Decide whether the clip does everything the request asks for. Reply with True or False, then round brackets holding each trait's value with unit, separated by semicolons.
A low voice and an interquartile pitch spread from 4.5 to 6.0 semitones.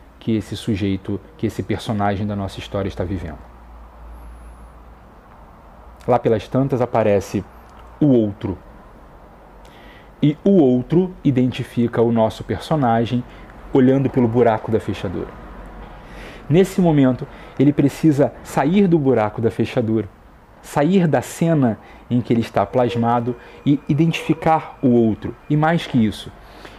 True (115 Hz; 5.2 semitones)